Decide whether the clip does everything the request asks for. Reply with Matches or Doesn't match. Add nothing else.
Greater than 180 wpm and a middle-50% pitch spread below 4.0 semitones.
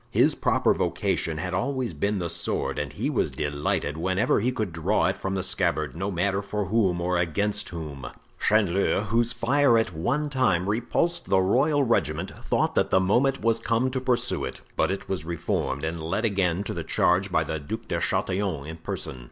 Doesn't match